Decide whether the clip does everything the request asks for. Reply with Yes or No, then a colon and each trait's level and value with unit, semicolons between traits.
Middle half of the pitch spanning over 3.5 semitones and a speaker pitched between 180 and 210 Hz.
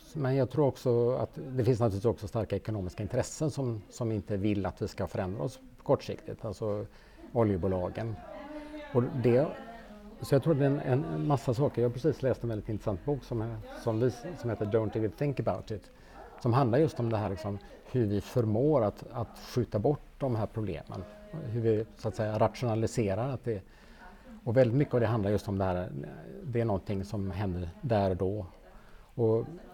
No: average, 4.5 semitones; low, 115 Hz